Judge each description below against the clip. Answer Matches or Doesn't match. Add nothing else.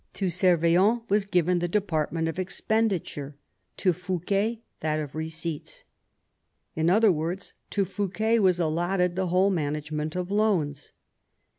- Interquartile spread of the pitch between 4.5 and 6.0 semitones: Doesn't match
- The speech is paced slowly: Matches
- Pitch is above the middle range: Doesn't match